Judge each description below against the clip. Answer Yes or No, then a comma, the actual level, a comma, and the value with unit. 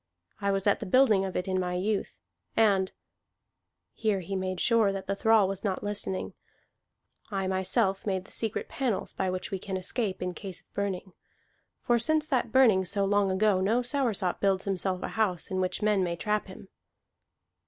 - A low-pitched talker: No, high, 195 Hz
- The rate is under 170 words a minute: No, average, 185 wpm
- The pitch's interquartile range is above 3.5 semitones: No, narrow, 2.4 semitones